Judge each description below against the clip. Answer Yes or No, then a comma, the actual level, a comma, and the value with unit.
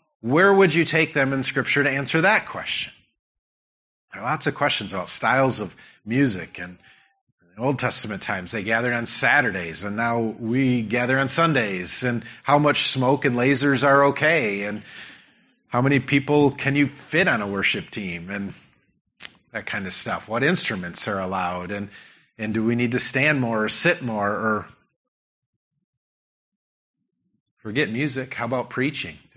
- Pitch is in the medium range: No, low, 125 Hz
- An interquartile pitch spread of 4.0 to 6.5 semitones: Yes, average, 5.2 semitones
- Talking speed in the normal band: Yes, average, 165 wpm